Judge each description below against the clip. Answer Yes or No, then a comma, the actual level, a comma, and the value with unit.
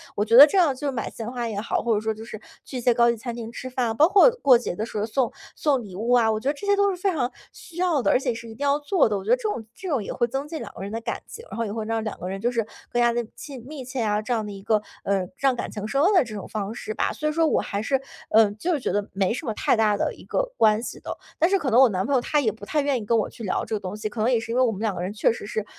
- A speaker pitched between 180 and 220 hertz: No, high, 235 Hz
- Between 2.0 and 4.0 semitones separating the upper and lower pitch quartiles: No, average, 4.4 semitones